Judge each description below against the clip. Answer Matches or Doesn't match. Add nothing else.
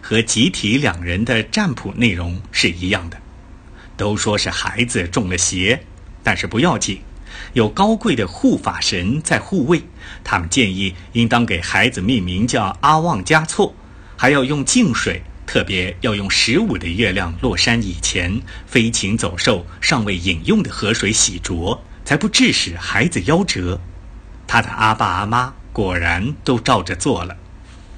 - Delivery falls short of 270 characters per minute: Matches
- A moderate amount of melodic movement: Matches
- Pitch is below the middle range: Matches